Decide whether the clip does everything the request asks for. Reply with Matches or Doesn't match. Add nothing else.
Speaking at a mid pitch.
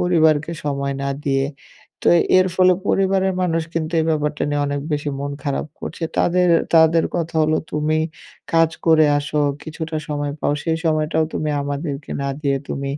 Matches